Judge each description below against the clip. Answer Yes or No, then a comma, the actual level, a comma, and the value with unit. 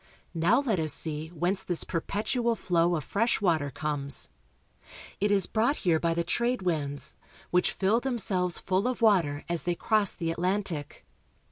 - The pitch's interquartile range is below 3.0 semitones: No, average, 4.5 semitones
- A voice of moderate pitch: Yes, medium, 180 Hz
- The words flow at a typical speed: Yes, average, 165 wpm